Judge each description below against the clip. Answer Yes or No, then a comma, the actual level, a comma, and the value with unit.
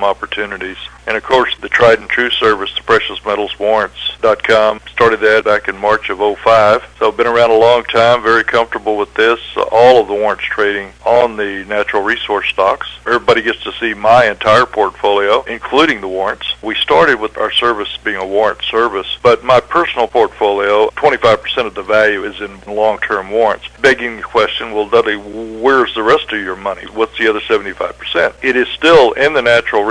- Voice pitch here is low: Yes, low, 110 Hz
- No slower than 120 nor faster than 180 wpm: No, average, 190 wpm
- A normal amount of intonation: No, narrow, 1.9 semitones